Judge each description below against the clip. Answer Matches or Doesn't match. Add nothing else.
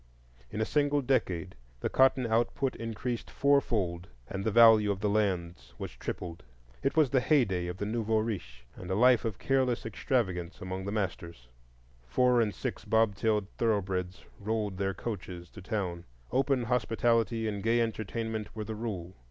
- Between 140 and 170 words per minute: Matches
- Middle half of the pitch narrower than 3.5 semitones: Doesn't match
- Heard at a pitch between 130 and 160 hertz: Doesn't match